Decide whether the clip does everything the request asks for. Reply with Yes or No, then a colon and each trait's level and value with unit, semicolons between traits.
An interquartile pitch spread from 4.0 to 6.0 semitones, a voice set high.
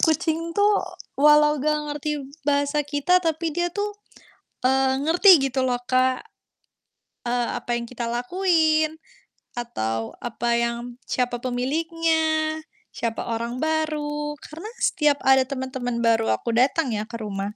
Yes: average, 4.5 semitones; very high, 280 Hz